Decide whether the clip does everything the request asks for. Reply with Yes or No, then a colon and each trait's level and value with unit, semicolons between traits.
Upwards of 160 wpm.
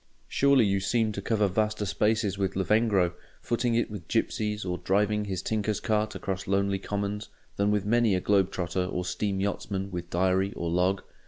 Yes: average, 180 wpm